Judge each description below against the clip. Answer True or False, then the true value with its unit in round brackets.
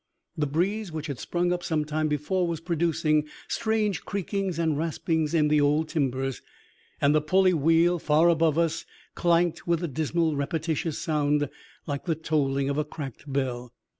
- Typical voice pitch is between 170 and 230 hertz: False (155 Hz)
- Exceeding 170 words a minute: False (165 wpm)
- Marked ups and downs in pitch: False (2.5 semitones)